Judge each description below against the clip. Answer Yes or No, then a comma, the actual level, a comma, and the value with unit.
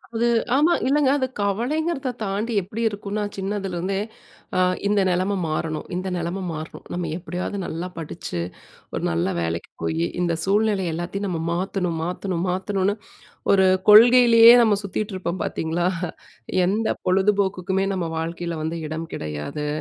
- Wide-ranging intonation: No, average, 3.6 semitones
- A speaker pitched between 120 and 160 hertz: No, high, 190 Hz